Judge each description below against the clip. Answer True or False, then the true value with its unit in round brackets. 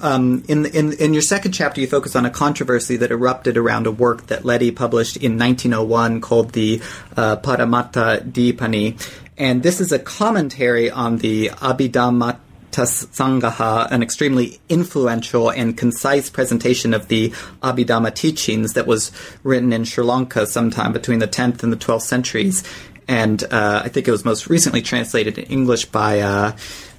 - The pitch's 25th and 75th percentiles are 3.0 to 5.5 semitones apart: False (2.4 semitones)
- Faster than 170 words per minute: False (160 wpm)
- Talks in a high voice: False (120 Hz)